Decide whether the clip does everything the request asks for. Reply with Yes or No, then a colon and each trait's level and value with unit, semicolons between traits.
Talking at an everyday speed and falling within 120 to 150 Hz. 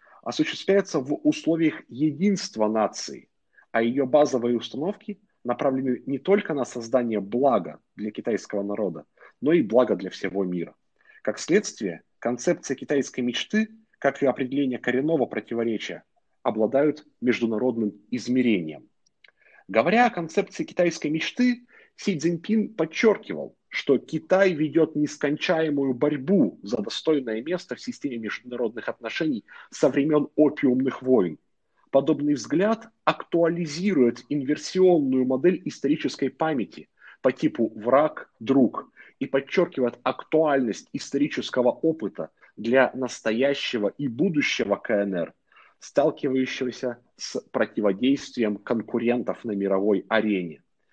No: slow, 105 wpm; low, 135 Hz